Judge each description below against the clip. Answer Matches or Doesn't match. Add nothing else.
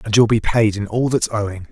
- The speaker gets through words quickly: Matches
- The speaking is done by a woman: Doesn't match